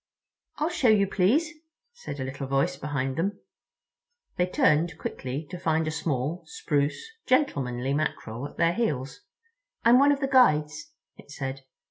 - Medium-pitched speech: Yes, medium, 160 Hz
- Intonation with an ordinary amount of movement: No, wide, 8.6 semitones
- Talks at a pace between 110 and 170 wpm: Yes, average, 150 wpm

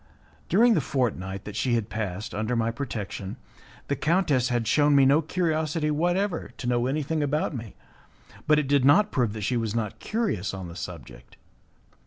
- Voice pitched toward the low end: Yes, low, 125 Hz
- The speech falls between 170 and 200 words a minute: Yes, average, 180 wpm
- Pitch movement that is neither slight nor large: No, wide, 6.2 semitones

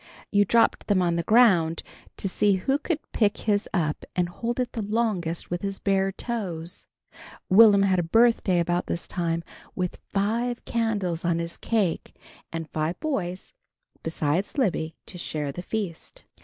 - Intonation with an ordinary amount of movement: Yes, average, 4.5 semitones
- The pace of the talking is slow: No, average, 160 wpm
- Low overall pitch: No, high, 190 Hz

